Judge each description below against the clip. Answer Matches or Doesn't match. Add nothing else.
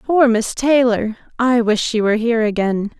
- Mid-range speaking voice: Doesn't match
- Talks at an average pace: Matches